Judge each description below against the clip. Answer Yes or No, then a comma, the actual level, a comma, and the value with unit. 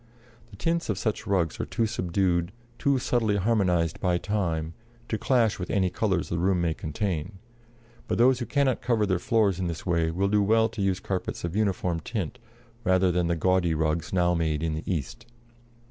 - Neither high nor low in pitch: No, very low, 95 Hz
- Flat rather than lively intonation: No, average, 4.0 semitones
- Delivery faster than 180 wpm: Yes, average, 190 wpm